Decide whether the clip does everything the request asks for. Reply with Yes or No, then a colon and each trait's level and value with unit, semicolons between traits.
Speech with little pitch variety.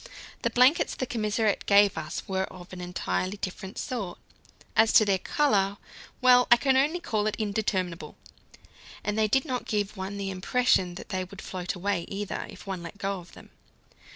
No: average, 3.1 semitones